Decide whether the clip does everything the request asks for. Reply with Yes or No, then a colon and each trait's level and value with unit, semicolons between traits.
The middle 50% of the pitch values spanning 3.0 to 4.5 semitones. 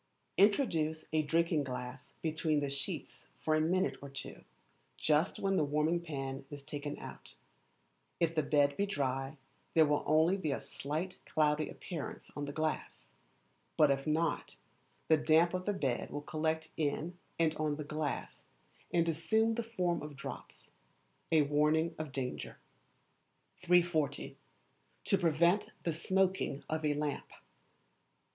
No: narrow, 2.6 semitones